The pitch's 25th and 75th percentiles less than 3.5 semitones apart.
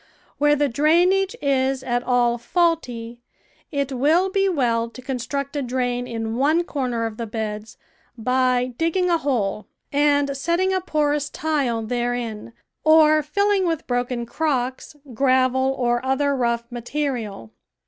No: average, 4.0 semitones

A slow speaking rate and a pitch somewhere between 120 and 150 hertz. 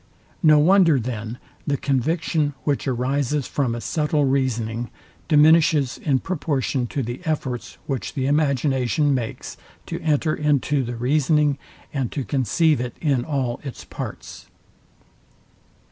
Yes: slow, 130 wpm; medium, 140 Hz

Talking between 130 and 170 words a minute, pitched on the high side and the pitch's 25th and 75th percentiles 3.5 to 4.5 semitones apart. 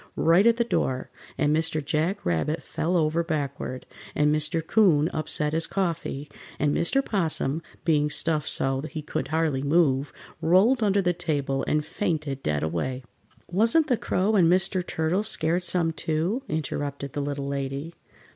No: average, 155 wpm; medium, 160 Hz; average, 3.8 semitones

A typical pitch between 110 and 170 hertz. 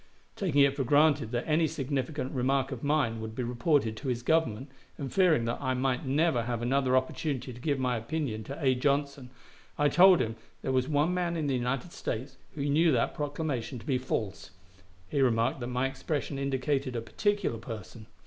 Yes: low, 135 Hz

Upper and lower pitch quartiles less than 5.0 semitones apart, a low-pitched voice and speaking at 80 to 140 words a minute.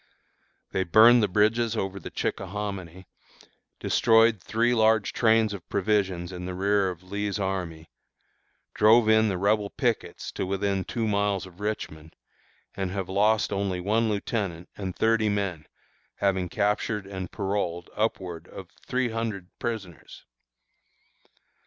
Yes: average, 2.7 semitones; low, 100 Hz; slow, 135 wpm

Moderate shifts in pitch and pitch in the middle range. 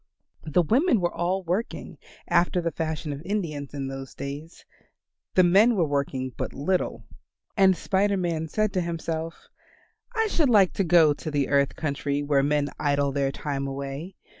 Yes: average, 4.7 semitones; medium, 160 Hz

